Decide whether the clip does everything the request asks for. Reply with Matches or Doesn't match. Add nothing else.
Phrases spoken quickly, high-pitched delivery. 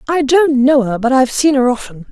Matches